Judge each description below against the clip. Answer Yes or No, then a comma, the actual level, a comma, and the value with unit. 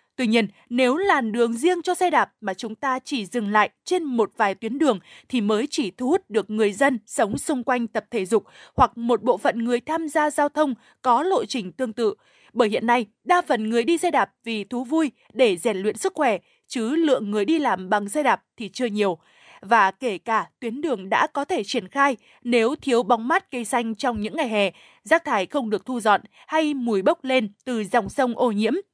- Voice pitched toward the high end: Yes, high, 245 Hz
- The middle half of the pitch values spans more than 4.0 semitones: Yes, average, 5.2 semitones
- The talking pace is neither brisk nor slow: Yes, average, 230 wpm